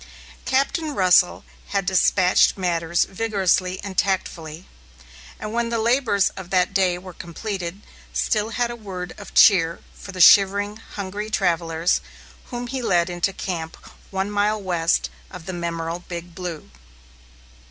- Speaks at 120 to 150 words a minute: Yes, average, 140 wpm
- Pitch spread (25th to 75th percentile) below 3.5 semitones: Yes, average, 3.1 semitones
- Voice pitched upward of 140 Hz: Yes, high, 190 Hz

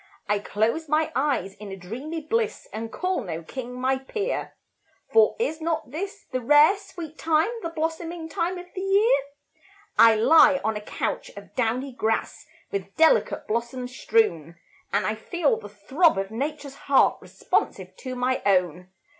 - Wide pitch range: Yes, wide, 7.0 semitones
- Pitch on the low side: No, very high, 270 Hz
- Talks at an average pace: Yes, average, 165 wpm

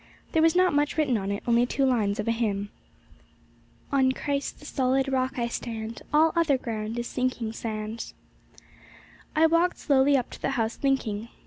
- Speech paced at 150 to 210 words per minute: Yes, average, 180 wpm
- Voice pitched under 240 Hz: No, very high, 255 Hz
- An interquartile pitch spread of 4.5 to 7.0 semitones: No, average, 4.0 semitones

